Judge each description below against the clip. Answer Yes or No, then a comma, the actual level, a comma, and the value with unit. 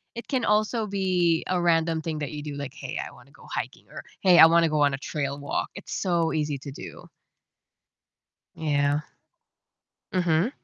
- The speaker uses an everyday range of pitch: Yes, average, 3.8 semitones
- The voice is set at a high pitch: No, medium, 165 Hz